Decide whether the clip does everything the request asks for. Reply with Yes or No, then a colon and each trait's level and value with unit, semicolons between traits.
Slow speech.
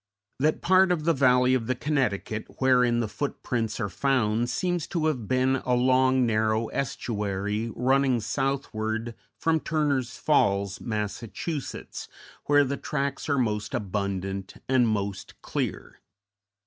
Yes: slow, 130 wpm